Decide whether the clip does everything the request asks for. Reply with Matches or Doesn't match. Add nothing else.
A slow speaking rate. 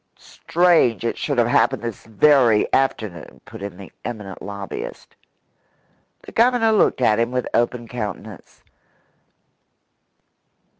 Matches